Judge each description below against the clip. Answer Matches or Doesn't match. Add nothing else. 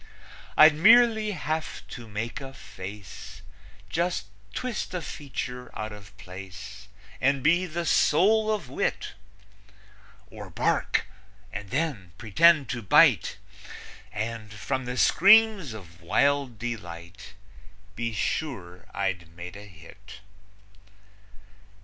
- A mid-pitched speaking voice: Doesn't match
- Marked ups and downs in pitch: Matches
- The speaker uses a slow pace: Matches